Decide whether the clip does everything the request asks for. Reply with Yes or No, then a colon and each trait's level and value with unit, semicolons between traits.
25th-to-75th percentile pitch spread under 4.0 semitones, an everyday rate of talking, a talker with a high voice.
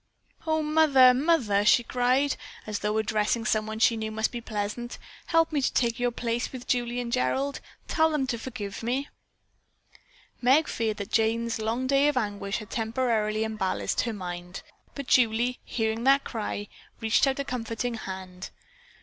Yes: average, 3.1 semitones; average, 165 wpm; high, 235 Hz